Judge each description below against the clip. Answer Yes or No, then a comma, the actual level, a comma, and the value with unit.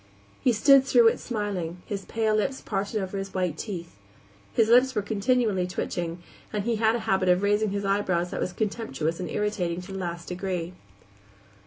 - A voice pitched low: No, high, 200 Hz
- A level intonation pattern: No, average, 3.4 semitones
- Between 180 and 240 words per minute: Yes, average, 185 wpm